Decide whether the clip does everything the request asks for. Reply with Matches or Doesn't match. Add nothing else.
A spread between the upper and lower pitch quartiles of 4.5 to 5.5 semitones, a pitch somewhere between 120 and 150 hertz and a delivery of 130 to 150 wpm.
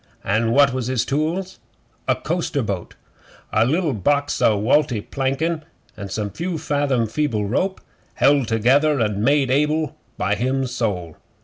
Matches